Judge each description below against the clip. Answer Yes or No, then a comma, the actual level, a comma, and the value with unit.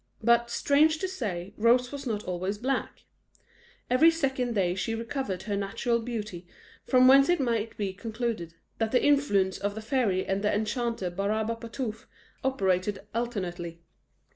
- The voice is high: Yes, high, 225 Hz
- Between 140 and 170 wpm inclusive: Yes, average, 145 wpm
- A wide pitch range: No, average, 4.2 semitones